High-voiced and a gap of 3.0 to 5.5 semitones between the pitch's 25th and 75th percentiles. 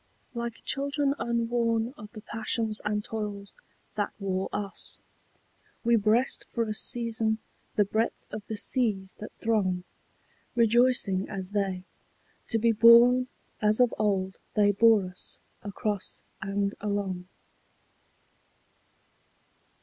No: high, 215 Hz; narrow, 2.5 semitones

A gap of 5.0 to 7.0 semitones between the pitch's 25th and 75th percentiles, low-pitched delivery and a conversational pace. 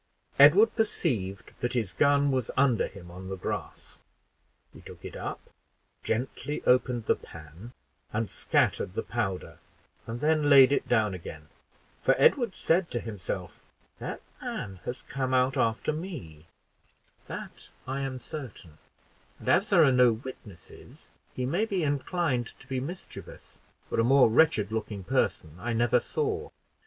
Yes: wide, 5.4 semitones; low, 125 Hz; average, 150 wpm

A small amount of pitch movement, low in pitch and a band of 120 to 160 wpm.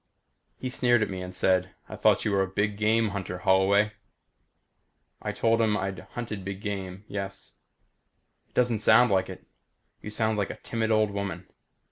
No: narrow, 2.3 semitones; low, 100 Hz; average, 175 wpm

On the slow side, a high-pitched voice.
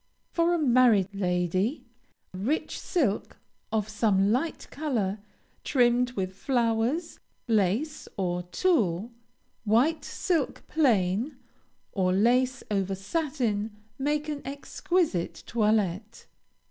Yes: slow, 95 wpm; high, 225 Hz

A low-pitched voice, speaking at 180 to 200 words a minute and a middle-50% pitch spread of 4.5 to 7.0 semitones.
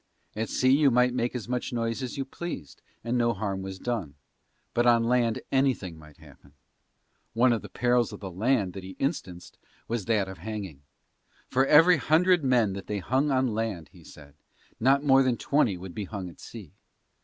Yes: low, 115 Hz; average, 195 wpm; average, 5.1 semitones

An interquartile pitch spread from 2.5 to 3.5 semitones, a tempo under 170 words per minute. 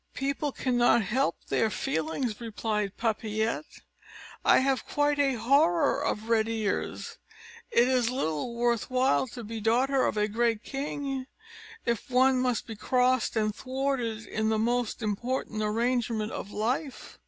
Yes: average, 3.2 semitones; average, 140 wpm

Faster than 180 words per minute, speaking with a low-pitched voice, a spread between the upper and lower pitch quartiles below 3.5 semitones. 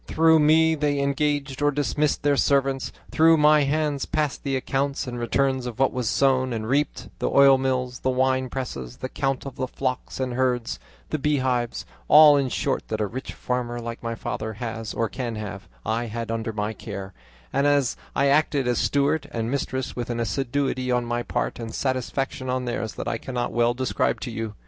Yes: average, 195 wpm; low, 130 Hz; average, 2.9 semitones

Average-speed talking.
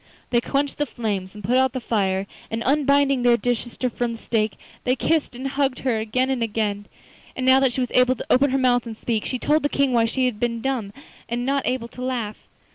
No: fast, 240 wpm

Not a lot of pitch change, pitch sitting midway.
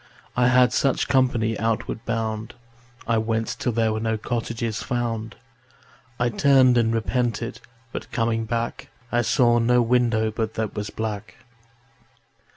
No: narrow, 1.5 semitones; low, 115 Hz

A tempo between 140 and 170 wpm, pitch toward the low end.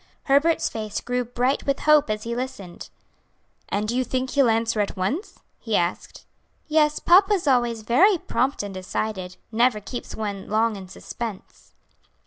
No: average, 160 wpm; high, 235 Hz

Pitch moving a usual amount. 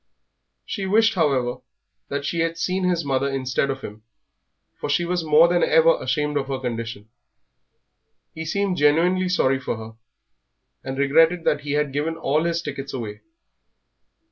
Yes: average, 4.3 semitones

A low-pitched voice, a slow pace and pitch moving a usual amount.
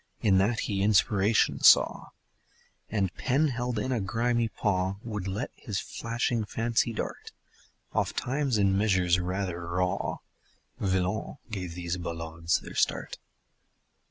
Yes: low, 100 Hz; slow, 125 wpm; average, 4.0 semitones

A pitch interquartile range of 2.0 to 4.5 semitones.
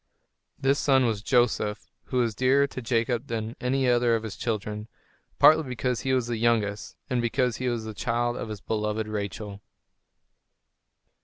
Yes: average, 2.7 semitones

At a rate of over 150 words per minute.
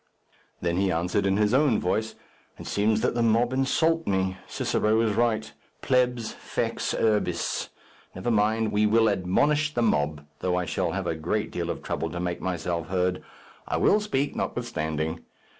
Yes: average, 170 wpm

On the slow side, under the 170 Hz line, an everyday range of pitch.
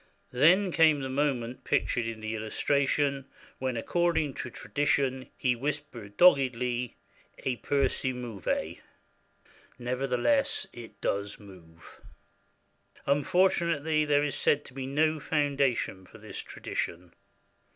Yes: slow, 115 wpm; low, 135 Hz; average, 3.5 semitones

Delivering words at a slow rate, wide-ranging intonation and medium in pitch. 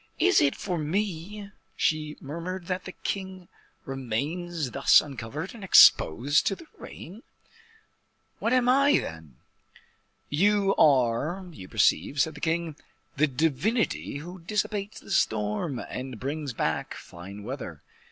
Yes: slow, 130 wpm; wide, 6.0 semitones; medium, 160 Hz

